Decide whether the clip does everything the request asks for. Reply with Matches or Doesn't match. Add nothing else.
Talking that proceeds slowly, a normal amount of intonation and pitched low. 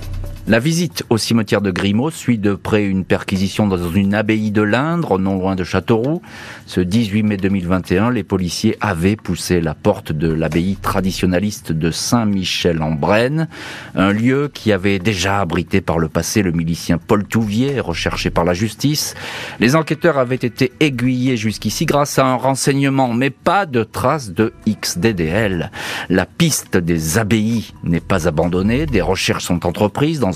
Doesn't match